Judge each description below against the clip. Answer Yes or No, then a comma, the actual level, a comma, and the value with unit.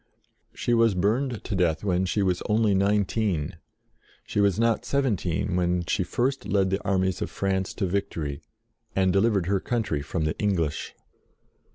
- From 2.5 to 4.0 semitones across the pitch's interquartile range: Yes, average, 2.8 semitones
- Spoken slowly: No, average, 165 wpm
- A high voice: No, very low, 95 Hz